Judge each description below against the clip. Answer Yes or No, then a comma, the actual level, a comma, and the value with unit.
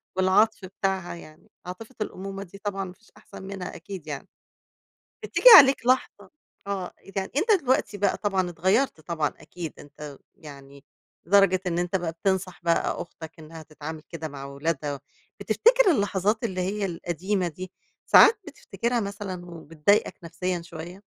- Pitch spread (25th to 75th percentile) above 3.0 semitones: Yes, average, 3.4 semitones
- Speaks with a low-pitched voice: No, medium, 185 Hz